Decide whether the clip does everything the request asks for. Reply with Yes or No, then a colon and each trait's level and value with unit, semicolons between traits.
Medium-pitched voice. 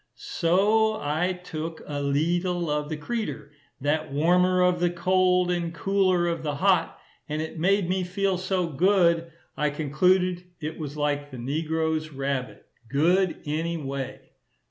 Yes: medium, 165 Hz